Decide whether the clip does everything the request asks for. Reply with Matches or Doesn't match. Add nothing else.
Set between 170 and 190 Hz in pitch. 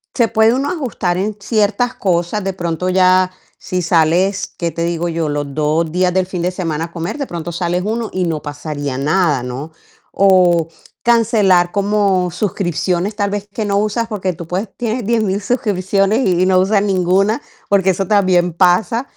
Matches